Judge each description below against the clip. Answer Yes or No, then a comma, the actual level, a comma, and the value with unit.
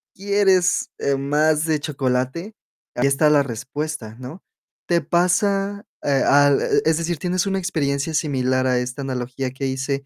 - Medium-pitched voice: Yes, medium, 145 Hz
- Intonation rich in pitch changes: No, average, 4.6 semitones